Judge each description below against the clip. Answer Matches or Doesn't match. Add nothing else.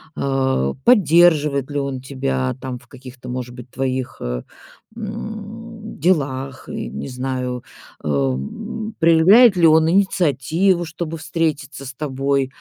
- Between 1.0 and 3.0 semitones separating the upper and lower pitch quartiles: Doesn't match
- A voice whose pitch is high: Doesn't match